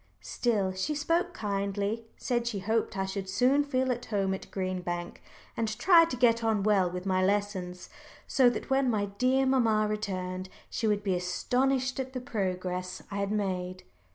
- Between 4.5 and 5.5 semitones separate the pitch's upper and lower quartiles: Yes, average, 4.8 semitones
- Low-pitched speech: No, high, 210 Hz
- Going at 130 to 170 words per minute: No, average, 180 wpm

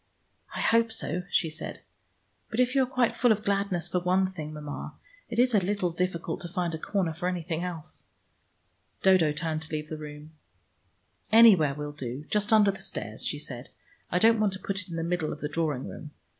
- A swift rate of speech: Yes, fast, 210 wpm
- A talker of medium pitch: Yes, medium, 175 Hz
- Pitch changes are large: No, average, 4.5 semitones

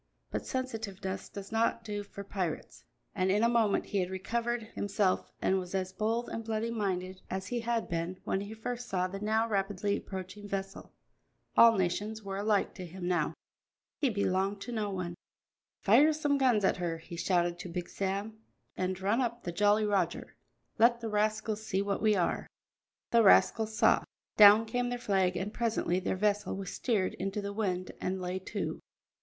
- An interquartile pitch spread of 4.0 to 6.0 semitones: No, average, 2.9 semitones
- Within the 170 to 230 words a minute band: Yes, average, 185 wpm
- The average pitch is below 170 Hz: No, high, 200 Hz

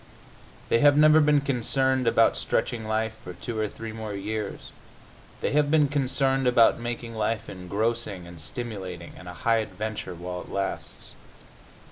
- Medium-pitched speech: No, low, 110 Hz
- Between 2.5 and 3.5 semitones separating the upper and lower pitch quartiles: No, average, 5.0 semitones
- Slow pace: No, average, 155 wpm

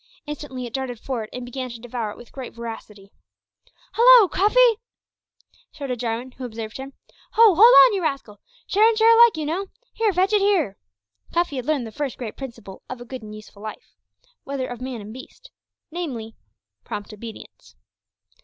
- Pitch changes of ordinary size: No, wide, 7.9 semitones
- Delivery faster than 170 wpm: Yes, average, 180 wpm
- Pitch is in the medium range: No, very high, 260 Hz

